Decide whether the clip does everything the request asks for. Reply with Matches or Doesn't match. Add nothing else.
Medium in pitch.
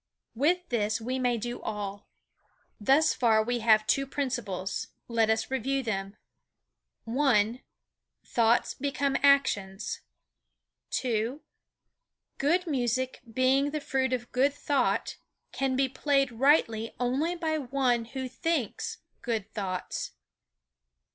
Doesn't match